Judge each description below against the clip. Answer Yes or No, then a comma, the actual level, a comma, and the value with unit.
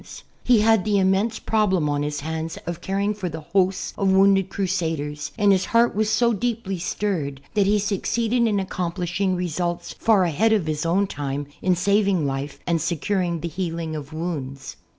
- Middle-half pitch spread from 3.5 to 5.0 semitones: Yes, average, 4.0 semitones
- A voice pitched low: No, medium, 185 Hz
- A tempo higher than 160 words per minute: Yes, average, 175 wpm